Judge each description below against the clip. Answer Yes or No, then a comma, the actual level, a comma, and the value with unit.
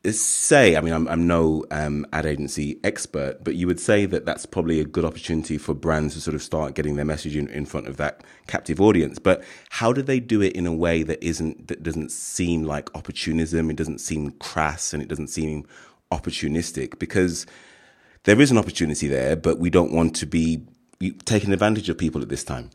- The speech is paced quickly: Yes, fast, 210 wpm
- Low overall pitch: Yes, very low, 80 Hz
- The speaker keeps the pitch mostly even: Yes, narrow, 2.1 semitones